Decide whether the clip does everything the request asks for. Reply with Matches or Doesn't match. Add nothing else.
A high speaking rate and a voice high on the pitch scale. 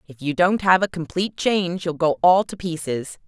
Doesn't match